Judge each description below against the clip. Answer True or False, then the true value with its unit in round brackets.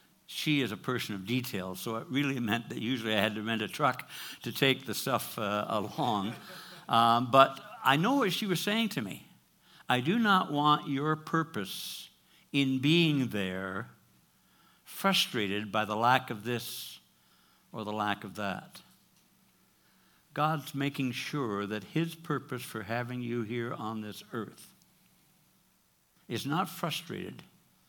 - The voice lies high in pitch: False (120 Hz)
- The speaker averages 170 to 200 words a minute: False (150 wpm)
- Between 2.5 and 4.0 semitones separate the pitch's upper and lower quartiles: False (4.9 semitones)